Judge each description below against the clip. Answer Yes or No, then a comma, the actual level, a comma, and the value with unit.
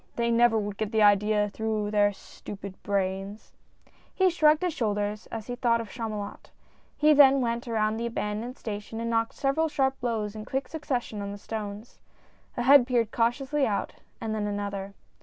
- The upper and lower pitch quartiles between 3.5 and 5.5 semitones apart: No, average, 3.0 semitones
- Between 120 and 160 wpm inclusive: No, average, 185 wpm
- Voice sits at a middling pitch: No, high, 225 Hz